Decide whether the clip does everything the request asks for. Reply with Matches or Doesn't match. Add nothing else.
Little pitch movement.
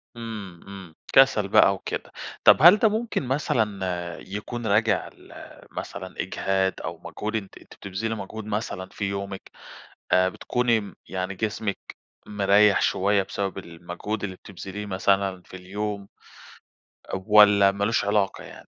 Matches